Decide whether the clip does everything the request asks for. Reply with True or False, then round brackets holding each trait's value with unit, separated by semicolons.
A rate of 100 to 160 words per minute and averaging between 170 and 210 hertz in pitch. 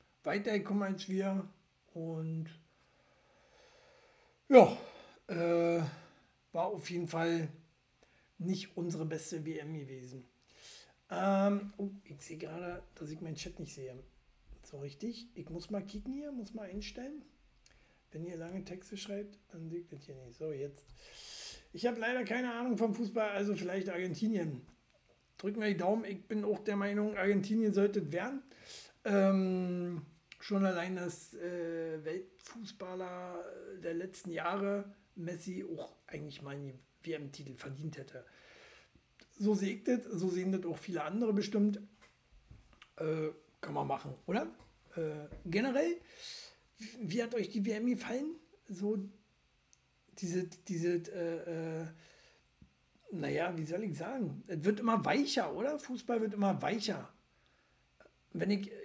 True (135 wpm; 185 Hz)